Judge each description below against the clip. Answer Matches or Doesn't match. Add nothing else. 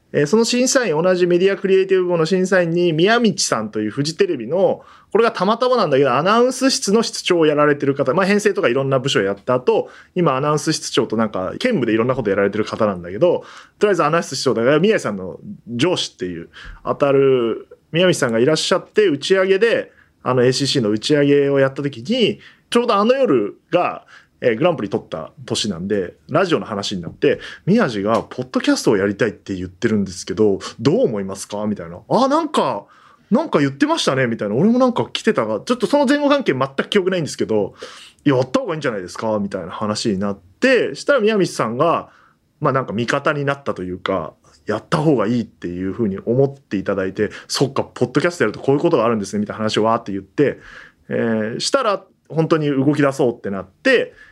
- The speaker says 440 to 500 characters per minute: Matches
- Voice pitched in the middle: Matches